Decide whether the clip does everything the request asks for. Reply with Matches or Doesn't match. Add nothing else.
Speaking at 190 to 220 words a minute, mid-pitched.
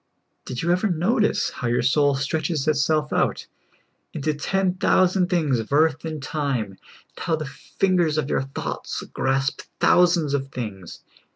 Doesn't match